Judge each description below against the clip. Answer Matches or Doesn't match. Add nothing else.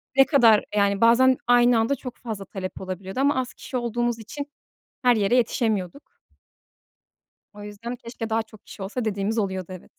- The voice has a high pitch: Matches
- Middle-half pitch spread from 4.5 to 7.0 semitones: Doesn't match